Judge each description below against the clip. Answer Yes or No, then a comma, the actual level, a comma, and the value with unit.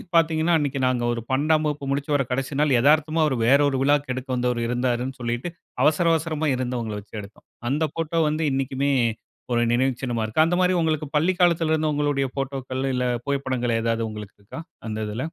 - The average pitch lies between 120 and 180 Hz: Yes, low, 135 Hz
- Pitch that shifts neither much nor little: Yes, average, 3.9 semitones